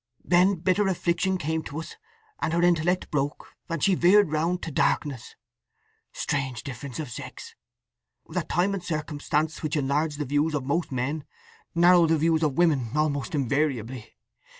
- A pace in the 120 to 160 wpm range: Yes, average, 155 wpm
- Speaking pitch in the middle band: Yes, medium, 155 Hz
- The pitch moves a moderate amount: Yes, average, 3.5 semitones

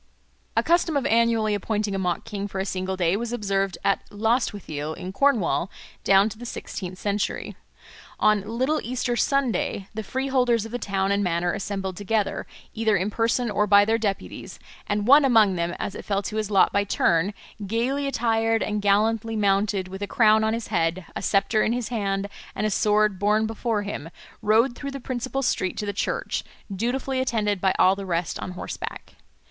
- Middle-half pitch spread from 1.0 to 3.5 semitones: Yes, average, 2.8 semitones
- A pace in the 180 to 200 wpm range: Yes, average, 190 wpm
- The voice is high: Yes, high, 210 Hz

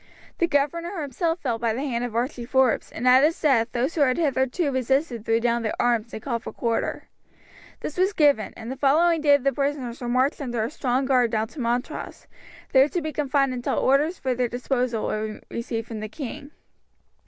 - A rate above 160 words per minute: Yes, fast, 205 wpm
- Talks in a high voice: Yes, very high, 260 Hz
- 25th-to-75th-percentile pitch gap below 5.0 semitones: Yes, average, 3.5 semitones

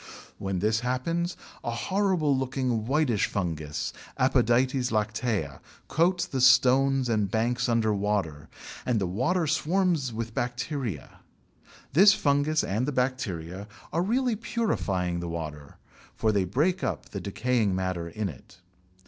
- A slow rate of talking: Yes, slow, 130 wpm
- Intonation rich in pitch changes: Yes, wide, 6.3 semitones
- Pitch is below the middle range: Yes, low, 120 Hz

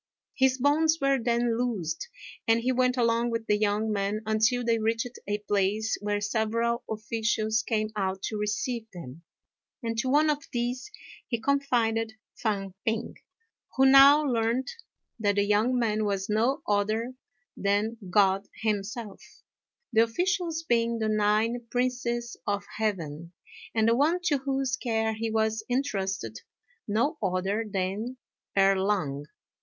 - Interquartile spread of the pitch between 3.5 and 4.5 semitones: No, average, 3.1 semitones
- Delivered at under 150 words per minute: Yes, average, 140 wpm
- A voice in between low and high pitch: No, high, 225 Hz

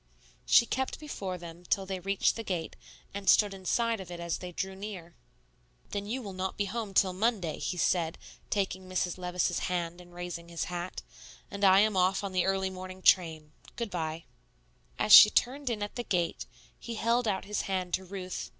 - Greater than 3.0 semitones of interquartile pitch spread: No, narrow, 2.6 semitones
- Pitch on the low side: No, high, 190 Hz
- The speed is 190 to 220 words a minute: Yes, average, 195 wpm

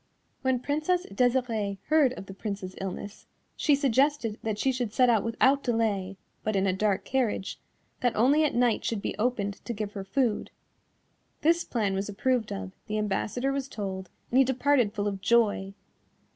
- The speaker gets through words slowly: No, average, 175 wpm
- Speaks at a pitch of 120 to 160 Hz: No, high, 225 Hz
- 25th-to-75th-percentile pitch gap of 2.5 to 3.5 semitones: No, average, 4.6 semitones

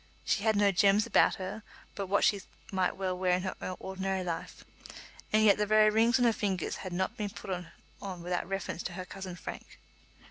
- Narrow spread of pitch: Yes, narrow, 2.1 semitones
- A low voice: No, high, 195 Hz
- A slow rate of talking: No, fast, 205 wpm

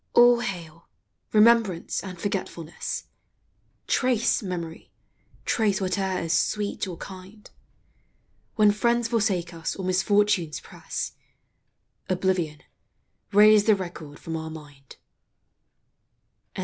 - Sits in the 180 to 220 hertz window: Yes, high, 190 Hz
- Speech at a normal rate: No, slow, 95 wpm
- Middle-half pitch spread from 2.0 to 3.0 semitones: No, average, 4.0 semitones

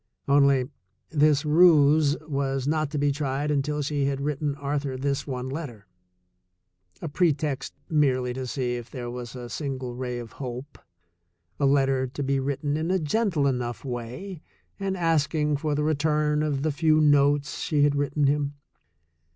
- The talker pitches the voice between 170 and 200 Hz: No, medium, 140 Hz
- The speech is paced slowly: No, average, 165 wpm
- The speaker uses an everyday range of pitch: No, narrow, 2.3 semitones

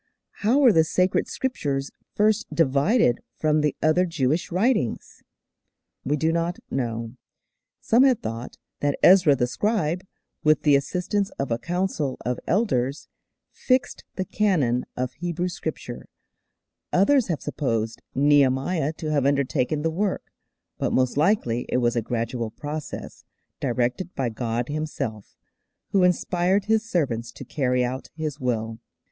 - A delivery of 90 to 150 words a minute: Yes, average, 140 wpm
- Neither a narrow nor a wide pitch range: No, wide, 6.3 semitones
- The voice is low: No, medium, 150 Hz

